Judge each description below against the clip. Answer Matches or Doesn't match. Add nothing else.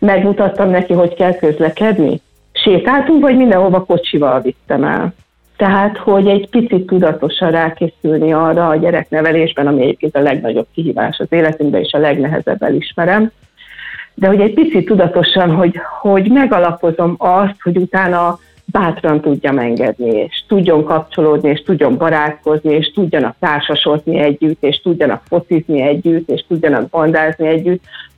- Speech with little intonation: Doesn't match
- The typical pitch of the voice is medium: Matches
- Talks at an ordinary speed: Matches